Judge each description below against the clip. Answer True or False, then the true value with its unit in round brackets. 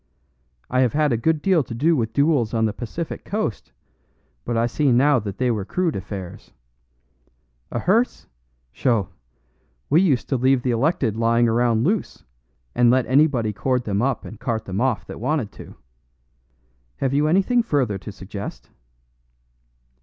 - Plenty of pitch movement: False (4.8 semitones)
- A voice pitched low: True (125 Hz)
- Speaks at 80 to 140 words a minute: False (160 wpm)